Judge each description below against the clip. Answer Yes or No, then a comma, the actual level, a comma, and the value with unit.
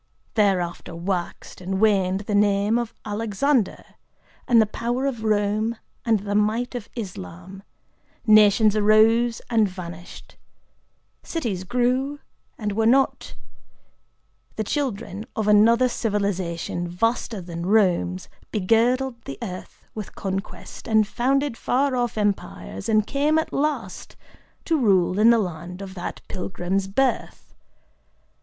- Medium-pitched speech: No, high, 215 Hz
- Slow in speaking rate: Yes, slow, 115 wpm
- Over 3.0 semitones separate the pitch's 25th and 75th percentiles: Yes, average, 3.7 semitones